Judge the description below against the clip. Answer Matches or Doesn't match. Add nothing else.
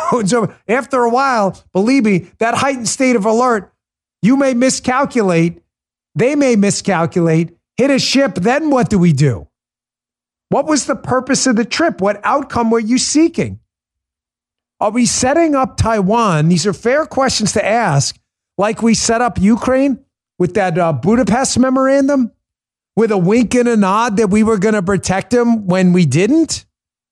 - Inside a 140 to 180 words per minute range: Matches